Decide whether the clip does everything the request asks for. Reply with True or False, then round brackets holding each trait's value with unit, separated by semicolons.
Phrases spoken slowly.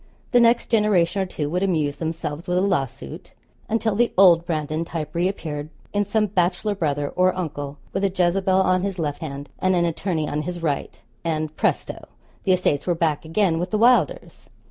False (190 wpm)